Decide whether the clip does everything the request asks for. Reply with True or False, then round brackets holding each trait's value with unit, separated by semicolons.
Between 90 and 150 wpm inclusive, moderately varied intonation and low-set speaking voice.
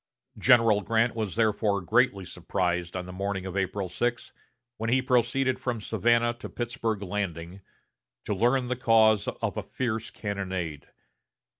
True (145 wpm; 3.9 semitones; 110 Hz)